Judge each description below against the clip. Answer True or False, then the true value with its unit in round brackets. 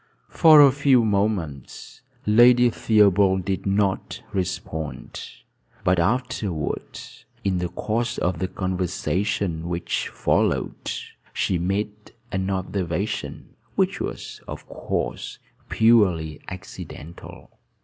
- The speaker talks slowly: True (100 wpm)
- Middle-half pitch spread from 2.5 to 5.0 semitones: True (3.5 semitones)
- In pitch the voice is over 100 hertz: False (95 Hz)